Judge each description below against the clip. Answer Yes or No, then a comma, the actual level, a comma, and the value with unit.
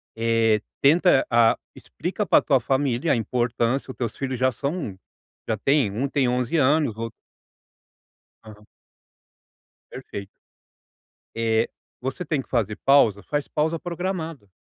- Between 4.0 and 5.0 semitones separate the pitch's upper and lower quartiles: Yes, average, 4.3 semitones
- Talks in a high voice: No, low, 130 Hz